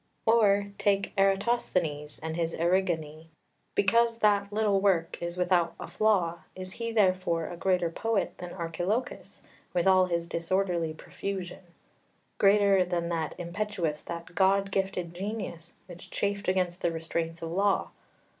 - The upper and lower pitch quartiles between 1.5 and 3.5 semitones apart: Yes, average, 2.9 semitones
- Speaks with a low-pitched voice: No, medium, 185 Hz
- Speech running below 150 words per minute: Yes, average, 140 wpm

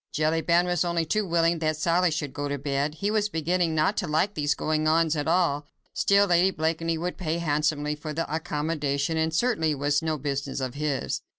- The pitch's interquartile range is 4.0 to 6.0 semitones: No, narrow, 2.5 semitones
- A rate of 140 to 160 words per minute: No, fast, 205 wpm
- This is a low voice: No, medium, 160 Hz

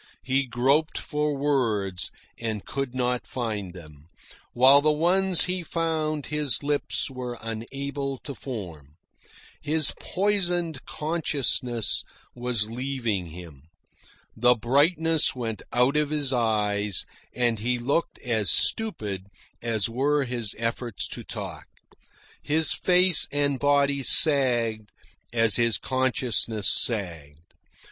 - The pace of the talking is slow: Yes, slow, 115 wpm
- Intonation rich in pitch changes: No, average, 4.8 semitones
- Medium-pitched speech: No, low, 125 Hz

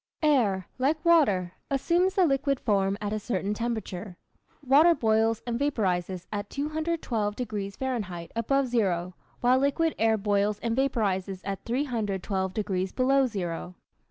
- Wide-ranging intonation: Yes, wide, 5.7 semitones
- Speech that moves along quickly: No, slow, 135 wpm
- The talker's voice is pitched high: Yes, high, 220 Hz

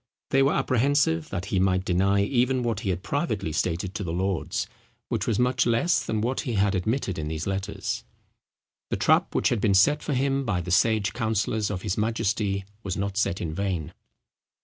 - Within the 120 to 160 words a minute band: No, average, 195 wpm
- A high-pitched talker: No, low, 100 Hz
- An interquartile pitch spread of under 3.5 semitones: No, average, 4.2 semitones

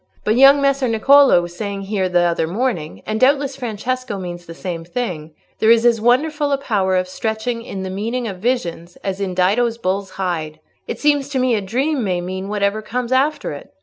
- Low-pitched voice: No, high, 215 Hz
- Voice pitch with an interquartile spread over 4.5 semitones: Yes, wide, 5.5 semitones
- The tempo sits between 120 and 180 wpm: No, average, 195 wpm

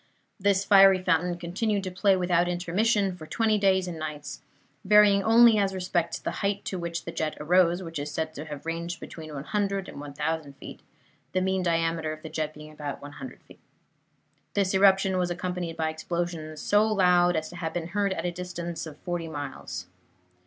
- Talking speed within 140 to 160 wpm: No, average, 190 wpm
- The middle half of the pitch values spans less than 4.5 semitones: Yes, average, 3.2 semitones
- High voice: No, medium, 175 Hz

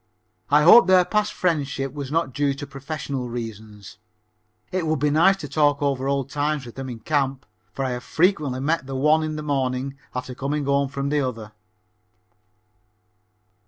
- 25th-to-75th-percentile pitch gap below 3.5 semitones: Yes, narrow, 2.6 semitones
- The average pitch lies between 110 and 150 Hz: Yes, medium, 140 Hz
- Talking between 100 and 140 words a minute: No, average, 175 wpm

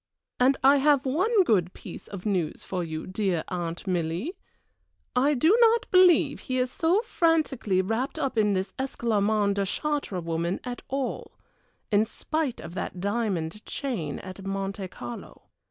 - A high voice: Yes, high, 215 Hz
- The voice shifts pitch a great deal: Yes, wide, 6.9 semitones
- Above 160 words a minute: No, average, 155 wpm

